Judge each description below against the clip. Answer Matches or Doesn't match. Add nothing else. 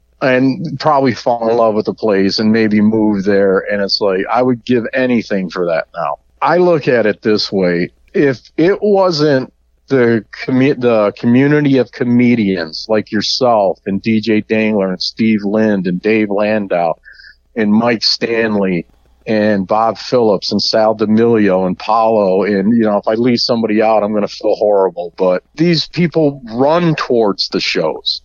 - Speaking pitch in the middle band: Doesn't match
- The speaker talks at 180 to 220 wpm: Doesn't match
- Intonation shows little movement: Doesn't match